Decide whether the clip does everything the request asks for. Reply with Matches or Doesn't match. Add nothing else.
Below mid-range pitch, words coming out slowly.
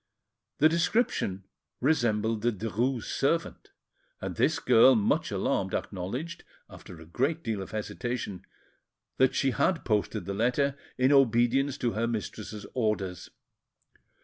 Matches